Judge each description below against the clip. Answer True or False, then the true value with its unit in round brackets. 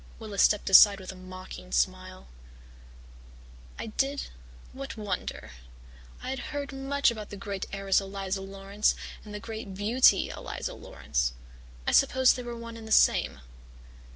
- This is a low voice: False (210 Hz)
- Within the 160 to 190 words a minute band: False (150 wpm)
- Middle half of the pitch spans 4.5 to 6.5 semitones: False (3.7 semitones)